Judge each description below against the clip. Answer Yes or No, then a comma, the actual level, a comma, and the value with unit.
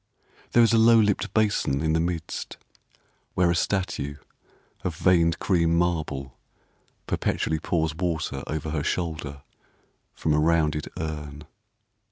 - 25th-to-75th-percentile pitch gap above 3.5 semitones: No, narrow, 2.6 semitones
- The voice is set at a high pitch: No, very low, 80 Hz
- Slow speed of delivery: Yes, slow, 130 wpm